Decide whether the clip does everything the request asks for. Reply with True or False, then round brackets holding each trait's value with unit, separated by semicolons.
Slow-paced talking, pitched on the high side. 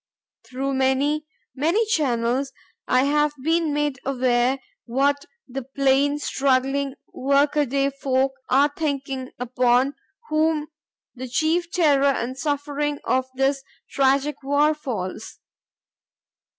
True (105 wpm; 275 Hz)